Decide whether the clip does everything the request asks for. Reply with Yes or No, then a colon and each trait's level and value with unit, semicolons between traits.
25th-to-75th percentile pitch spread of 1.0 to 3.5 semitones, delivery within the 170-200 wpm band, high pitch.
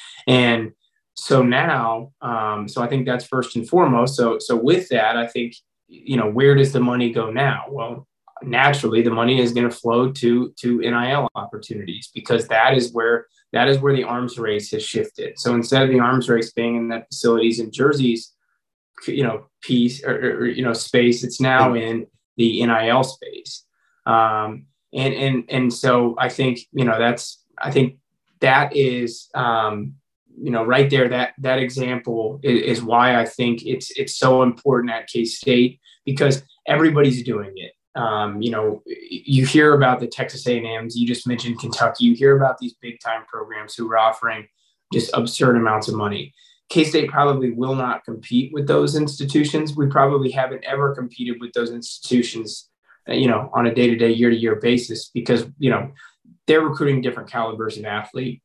No: narrow, 2.5 semitones; average, 185 wpm; low, 125 Hz